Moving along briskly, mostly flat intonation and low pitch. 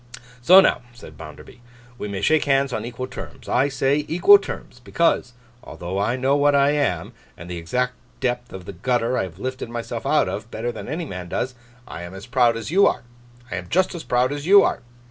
No: fast, 220 wpm; wide, 5.5 semitones; low, 125 Hz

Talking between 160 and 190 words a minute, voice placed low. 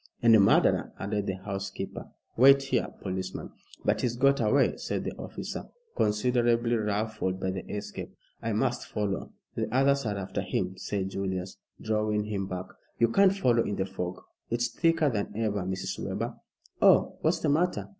Yes: average, 165 wpm; low, 105 Hz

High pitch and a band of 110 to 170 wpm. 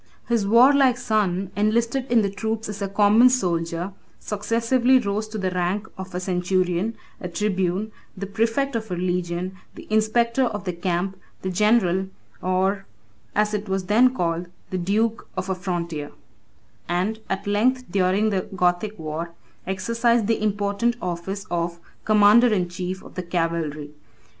Yes: high, 200 Hz; average, 150 wpm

